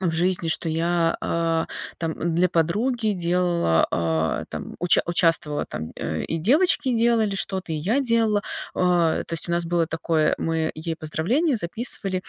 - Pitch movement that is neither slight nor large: Yes, average, 3.6 semitones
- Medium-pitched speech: Yes, medium, 170 Hz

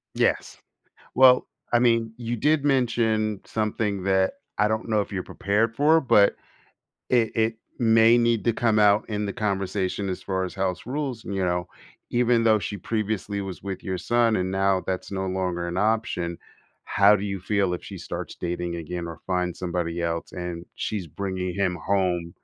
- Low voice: Yes, low, 100 Hz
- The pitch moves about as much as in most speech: Yes, average, 3.5 semitones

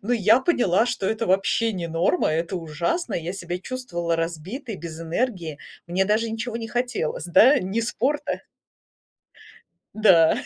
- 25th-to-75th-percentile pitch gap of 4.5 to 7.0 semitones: Yes, wide, 5.6 semitones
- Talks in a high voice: Yes, high, 195 Hz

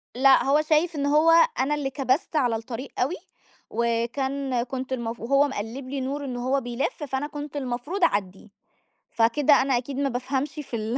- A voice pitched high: Yes, very high, 265 Hz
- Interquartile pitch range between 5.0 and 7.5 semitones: No, average, 3.0 semitones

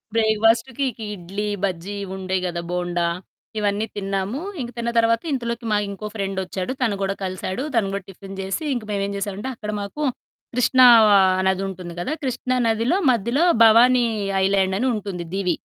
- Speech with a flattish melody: No, average, 3.5 semitones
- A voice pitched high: Yes, high, 200 Hz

